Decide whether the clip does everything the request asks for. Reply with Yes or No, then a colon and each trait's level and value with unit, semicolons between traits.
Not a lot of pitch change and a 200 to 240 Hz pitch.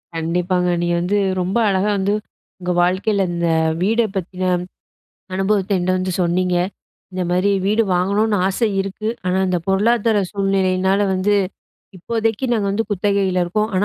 No: narrow, 2.2 semitones; high, 190 Hz